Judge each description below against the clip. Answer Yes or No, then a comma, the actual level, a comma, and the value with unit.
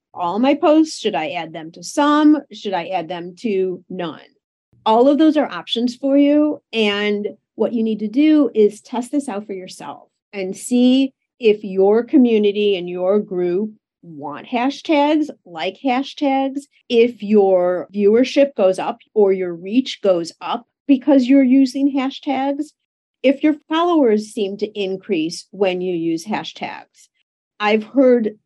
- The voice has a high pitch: Yes, high, 220 Hz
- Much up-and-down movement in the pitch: Yes, wide, 6.3 semitones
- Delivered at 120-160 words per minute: Yes, average, 150 wpm